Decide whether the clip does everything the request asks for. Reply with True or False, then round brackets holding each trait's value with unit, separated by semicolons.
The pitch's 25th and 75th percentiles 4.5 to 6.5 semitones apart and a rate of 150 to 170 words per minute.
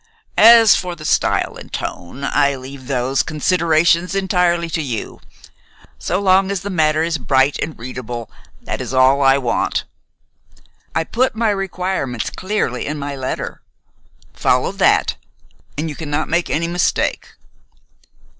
False (5.1 semitones; 140 wpm)